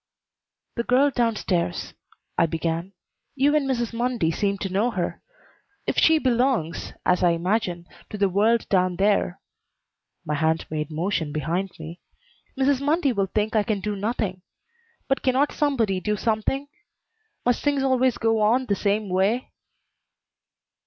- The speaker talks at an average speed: Yes, average, 150 wpm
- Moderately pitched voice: No, high, 210 Hz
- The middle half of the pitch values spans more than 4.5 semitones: Yes, wide, 5.5 semitones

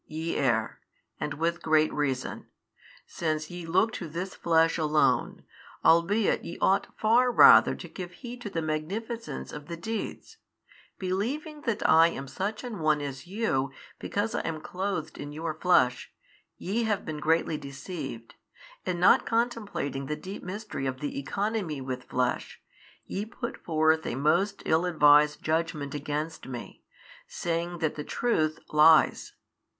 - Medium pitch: Yes, medium, 165 Hz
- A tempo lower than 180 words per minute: Yes, average, 150 wpm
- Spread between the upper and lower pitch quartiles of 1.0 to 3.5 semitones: No, average, 4.9 semitones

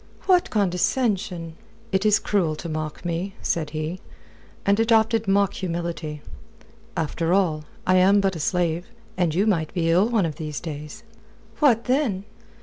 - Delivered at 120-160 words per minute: Yes, average, 150 wpm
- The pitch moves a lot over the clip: No, average, 3.8 semitones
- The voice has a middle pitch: Yes, medium, 180 Hz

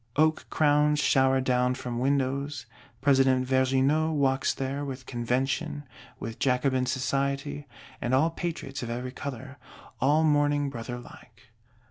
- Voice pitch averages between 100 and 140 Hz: Yes, low, 135 Hz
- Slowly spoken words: Yes, slow, 125 wpm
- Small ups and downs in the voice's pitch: Yes, narrow, 2.1 semitones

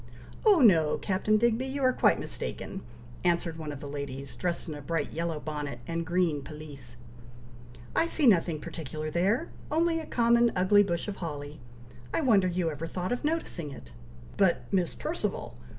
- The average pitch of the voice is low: No, medium, 175 Hz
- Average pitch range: No, wide, 6.8 semitones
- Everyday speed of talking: Yes, average, 170 wpm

